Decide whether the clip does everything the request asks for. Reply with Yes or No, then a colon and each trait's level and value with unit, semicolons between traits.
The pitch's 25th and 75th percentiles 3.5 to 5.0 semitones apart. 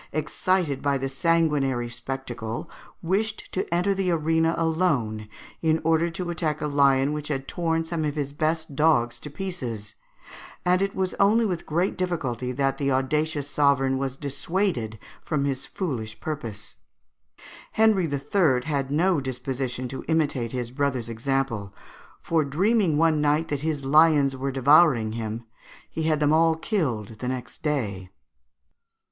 Yes: average, 3.8 semitones